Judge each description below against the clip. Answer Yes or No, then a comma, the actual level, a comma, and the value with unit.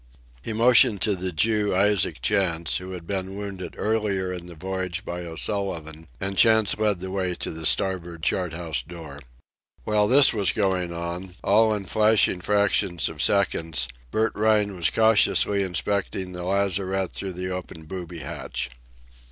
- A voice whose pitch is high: No, very low, 95 Hz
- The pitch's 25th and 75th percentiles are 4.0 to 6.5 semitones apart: No, average, 2.9 semitones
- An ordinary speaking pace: Yes, average, 160 wpm